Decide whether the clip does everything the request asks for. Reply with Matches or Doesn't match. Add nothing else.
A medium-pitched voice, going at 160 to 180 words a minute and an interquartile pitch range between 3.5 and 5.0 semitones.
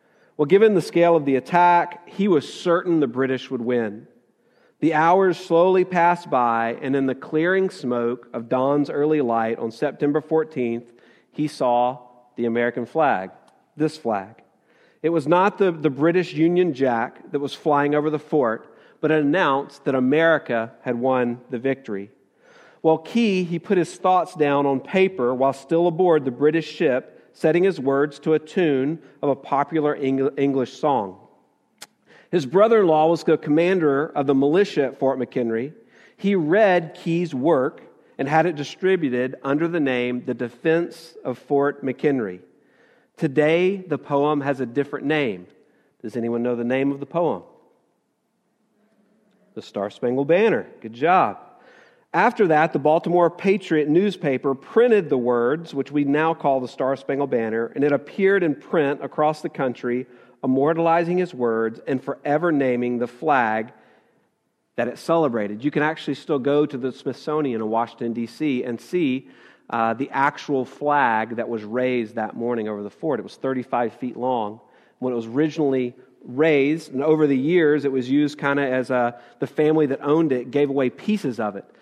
Matches